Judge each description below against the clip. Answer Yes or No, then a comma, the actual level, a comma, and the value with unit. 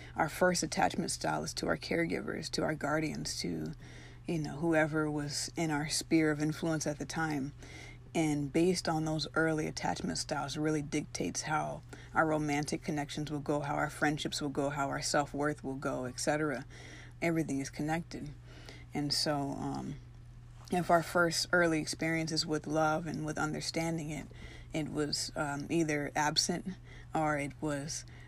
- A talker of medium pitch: Yes, medium, 150 Hz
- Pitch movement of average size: No, narrow, 2.0 semitones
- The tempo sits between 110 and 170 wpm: Yes, average, 160 wpm